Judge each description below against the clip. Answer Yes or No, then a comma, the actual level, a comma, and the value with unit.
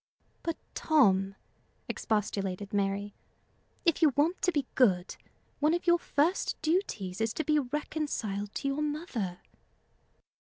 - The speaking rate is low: Yes, slow, 125 wpm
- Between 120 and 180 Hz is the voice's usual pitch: No, very high, 275 Hz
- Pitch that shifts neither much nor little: No, wide, 7.7 semitones